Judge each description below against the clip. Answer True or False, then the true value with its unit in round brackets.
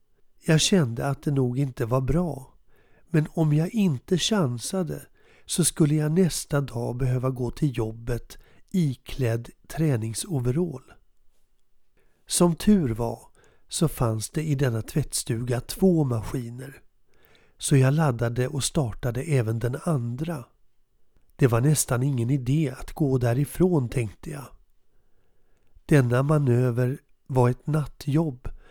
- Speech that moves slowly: True (120 wpm)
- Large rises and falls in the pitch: False (4.3 semitones)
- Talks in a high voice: False (135 Hz)